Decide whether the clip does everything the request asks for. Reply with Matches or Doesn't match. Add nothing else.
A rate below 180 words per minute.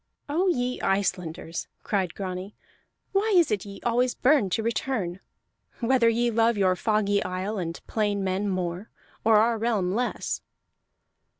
Matches